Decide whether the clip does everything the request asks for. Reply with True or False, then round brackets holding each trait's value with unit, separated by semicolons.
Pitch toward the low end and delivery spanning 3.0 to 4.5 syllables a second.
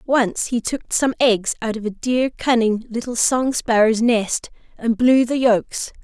False (235 Hz; 4.0 syllables/s)